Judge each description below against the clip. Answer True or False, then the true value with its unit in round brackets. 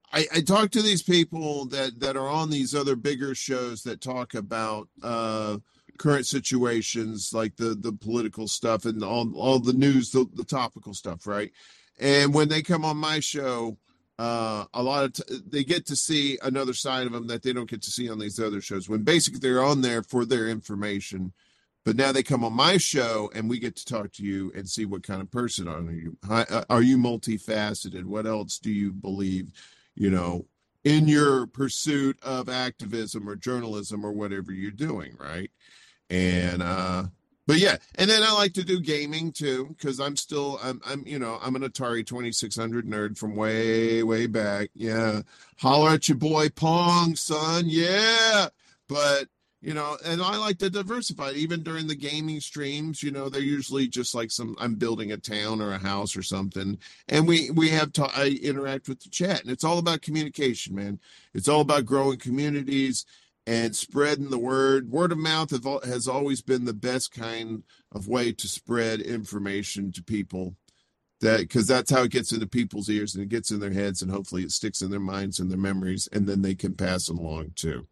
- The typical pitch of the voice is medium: False (120 Hz)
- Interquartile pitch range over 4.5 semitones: True (5.4 semitones)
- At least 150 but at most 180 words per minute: False (195 wpm)